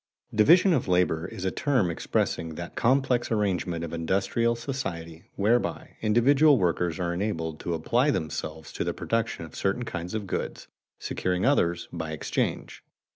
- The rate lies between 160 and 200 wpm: No, average, 150 wpm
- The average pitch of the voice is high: No, very low, 95 Hz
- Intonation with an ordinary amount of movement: No, wide, 6.1 semitones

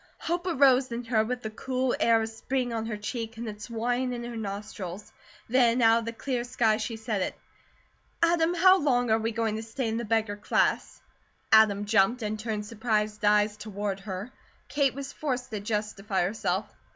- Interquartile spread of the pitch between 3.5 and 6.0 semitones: No, average, 2.7 semitones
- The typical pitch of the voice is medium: No, high, 225 Hz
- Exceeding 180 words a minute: Yes, average, 190 wpm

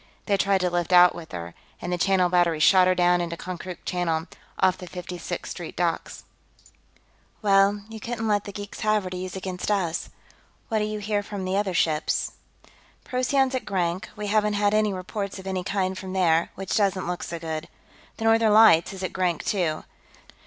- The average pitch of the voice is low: No, high, 190 Hz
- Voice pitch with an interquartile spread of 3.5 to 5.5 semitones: No, average, 2.7 semitones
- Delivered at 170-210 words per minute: Yes, average, 200 wpm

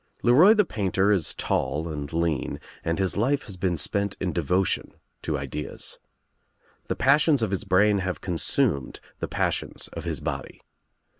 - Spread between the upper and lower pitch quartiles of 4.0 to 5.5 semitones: Yes, average, 4.4 semitones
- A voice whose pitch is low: Yes, very low, 95 Hz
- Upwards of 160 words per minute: No, average, 155 wpm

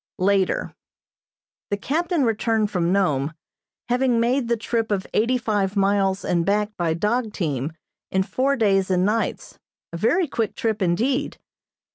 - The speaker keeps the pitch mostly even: No, average, 3.9 semitones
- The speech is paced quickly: No, average, 145 wpm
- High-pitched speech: Yes, high, 210 Hz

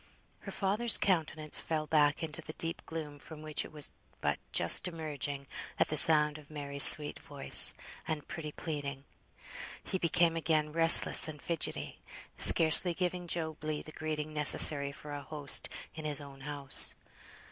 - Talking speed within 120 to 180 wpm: Yes, average, 160 wpm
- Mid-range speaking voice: Yes, medium, 155 Hz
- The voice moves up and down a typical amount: No, narrow, 1.8 semitones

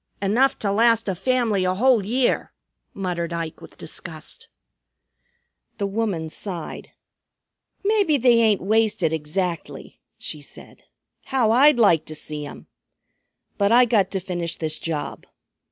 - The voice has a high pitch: Yes, high, 200 Hz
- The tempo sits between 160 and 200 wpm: No, slow, 135 wpm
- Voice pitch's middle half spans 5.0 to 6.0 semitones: Yes, wide, 5.4 semitones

